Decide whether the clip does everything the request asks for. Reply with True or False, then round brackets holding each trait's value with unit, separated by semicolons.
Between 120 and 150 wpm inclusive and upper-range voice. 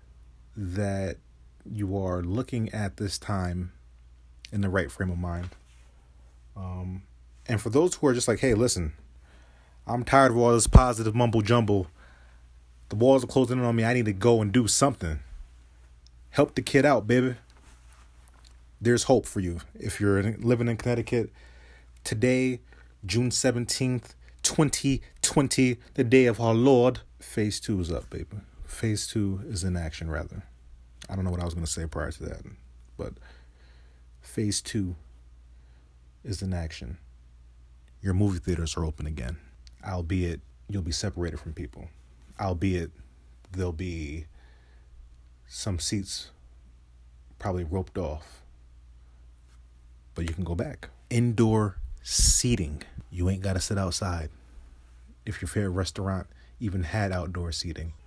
False (145 wpm; 90 Hz)